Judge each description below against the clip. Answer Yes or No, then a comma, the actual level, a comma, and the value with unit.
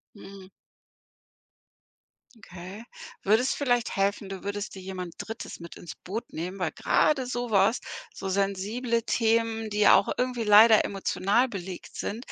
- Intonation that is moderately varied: Yes, average, 3.1 semitones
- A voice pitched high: Yes, high, 205 Hz